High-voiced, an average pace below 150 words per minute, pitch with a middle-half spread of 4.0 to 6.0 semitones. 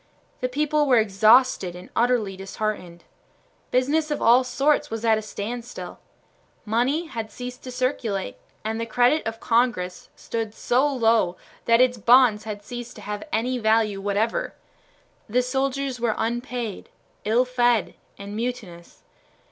No: high, 235 Hz; average, 140 wpm; average, 2.8 semitones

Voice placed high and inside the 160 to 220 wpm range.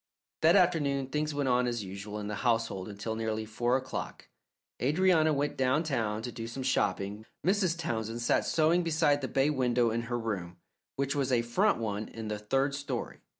No: low, 125 Hz; average, 185 wpm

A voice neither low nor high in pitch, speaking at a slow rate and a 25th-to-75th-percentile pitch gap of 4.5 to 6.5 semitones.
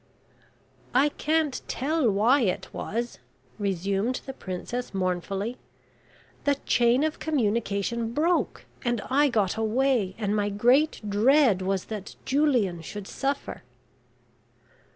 No: high, 230 Hz; slow, 110 wpm; average, 5.3 semitones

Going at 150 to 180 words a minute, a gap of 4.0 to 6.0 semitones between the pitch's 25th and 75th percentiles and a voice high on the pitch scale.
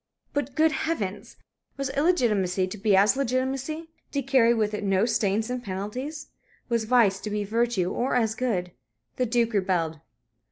Yes: average, 160 wpm; average, 4.7 semitones; high, 230 Hz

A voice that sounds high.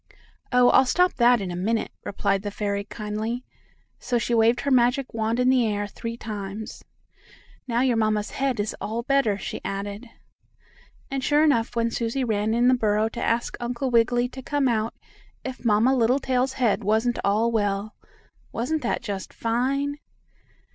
Yes: high, 230 Hz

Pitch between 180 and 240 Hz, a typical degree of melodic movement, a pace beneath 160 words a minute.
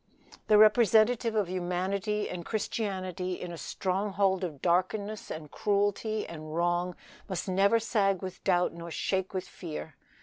Yes: high, 190 Hz; average, 3.0 semitones; average, 140 wpm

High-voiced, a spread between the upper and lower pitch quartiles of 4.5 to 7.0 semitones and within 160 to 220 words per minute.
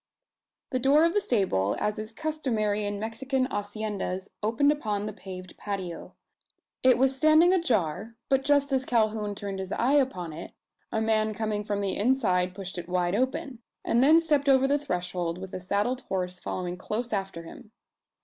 Yes: high, 215 Hz; wide, 5.6 semitones; average, 175 wpm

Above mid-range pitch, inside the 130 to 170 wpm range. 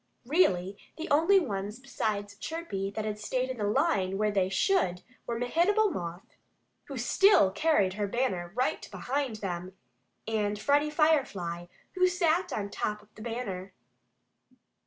Yes: high, 215 Hz; average, 145 wpm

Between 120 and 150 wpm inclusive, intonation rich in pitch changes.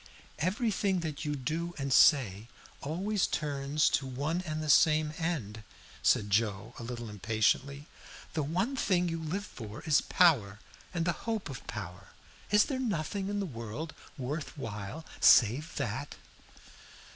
Yes: average, 145 wpm; wide, 6.7 semitones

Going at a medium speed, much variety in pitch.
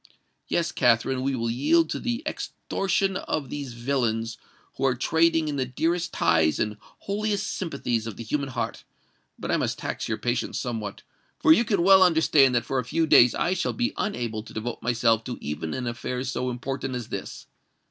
Yes: average, 190 wpm; wide, 6.0 semitones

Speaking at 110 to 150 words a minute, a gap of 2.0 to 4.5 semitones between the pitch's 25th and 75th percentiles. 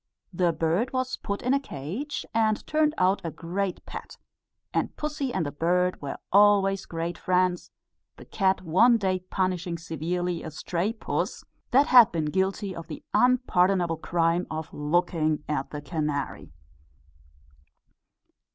Yes: average, 140 wpm; average, 3.9 semitones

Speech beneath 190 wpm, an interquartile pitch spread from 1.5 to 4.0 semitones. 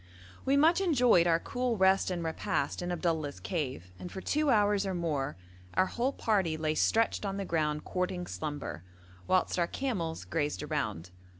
No: average, 170 wpm; average, 5.0 semitones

